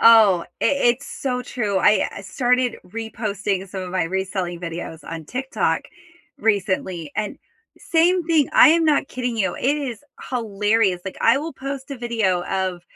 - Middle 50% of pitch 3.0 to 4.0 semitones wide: No, average, 5.3 semitones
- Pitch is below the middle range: No, high, 220 Hz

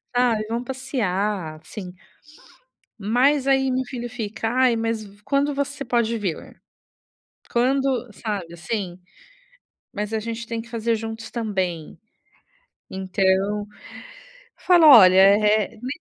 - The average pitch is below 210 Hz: No, high, 225 Hz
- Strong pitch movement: No, average, 3.7 semitones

